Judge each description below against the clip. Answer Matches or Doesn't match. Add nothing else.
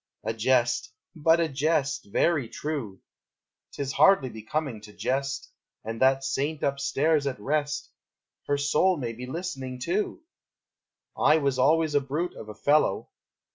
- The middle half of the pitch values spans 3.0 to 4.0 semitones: Matches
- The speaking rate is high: Doesn't match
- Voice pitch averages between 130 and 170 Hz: Matches